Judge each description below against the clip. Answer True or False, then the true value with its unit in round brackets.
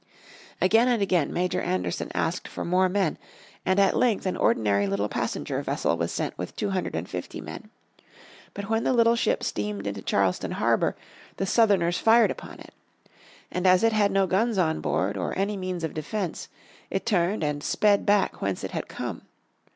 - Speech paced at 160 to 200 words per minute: True (185 wpm)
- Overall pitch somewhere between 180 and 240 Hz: True (185 Hz)